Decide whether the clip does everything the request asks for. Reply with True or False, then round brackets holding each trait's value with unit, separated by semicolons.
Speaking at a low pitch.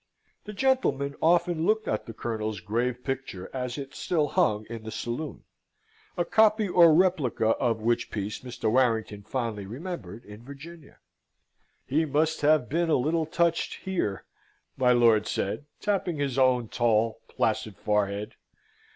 True (130 Hz)